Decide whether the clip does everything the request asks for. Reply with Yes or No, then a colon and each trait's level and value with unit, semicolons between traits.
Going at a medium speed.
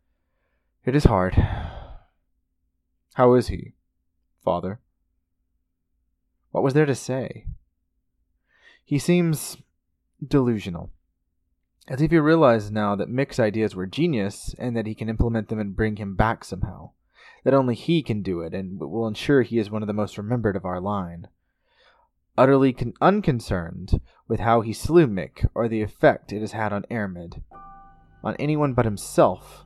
Yes: average, 150 wpm